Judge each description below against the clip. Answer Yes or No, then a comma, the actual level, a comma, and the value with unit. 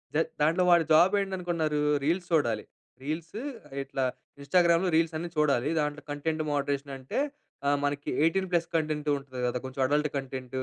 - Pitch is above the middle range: No, medium, 150 Hz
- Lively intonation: No, average, 3.2 semitones